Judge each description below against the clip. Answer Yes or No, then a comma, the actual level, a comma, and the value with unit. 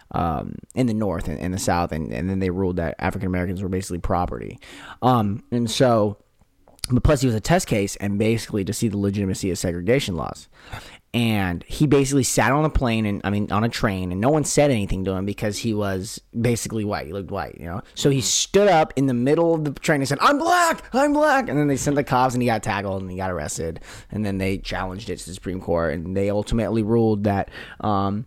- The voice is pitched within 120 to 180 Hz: No, low, 105 Hz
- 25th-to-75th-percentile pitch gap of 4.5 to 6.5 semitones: Yes, average, 5.1 semitones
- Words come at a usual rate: No, fast, 240 wpm